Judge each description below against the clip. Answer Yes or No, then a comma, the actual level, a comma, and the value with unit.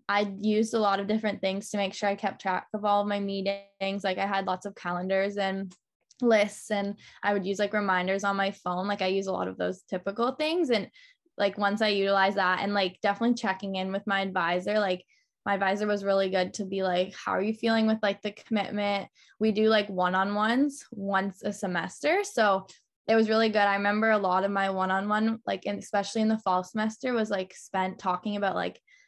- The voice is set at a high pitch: Yes, high, 200 Hz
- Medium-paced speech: No, fast, 230 wpm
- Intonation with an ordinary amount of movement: No, narrow, 1.8 semitones